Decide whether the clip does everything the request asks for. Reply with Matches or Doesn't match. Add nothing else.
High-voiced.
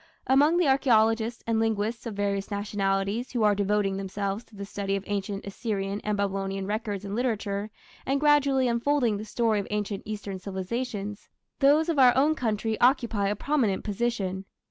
Matches